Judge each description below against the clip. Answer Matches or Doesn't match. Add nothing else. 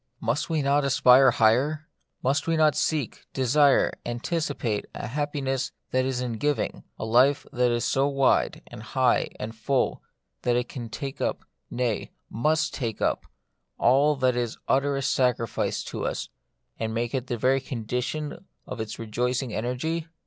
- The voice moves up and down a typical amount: Matches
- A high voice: Doesn't match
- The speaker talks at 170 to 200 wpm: Doesn't match